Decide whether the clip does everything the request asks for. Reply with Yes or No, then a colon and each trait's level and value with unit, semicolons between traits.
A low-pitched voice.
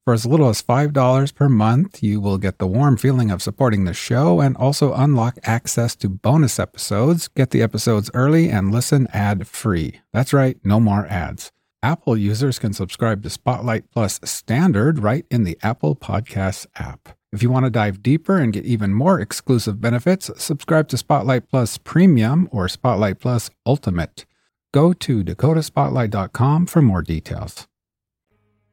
Yes: low, 120 Hz